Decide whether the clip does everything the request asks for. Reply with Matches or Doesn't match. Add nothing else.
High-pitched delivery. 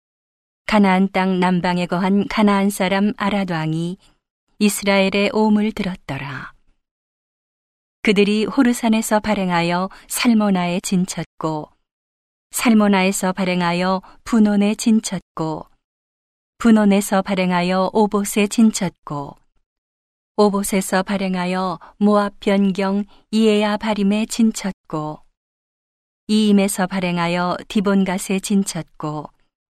Matches